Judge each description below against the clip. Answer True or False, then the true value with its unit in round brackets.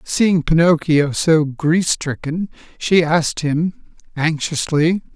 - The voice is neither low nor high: True (160 Hz)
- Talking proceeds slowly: True (105 wpm)